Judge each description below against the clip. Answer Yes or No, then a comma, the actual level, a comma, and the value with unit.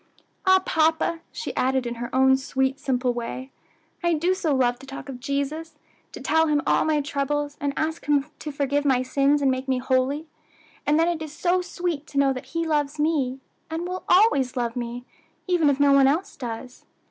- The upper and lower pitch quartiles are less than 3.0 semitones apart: No, average, 3.4 semitones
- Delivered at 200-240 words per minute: Yes, fast, 205 wpm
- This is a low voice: No, very high, 285 Hz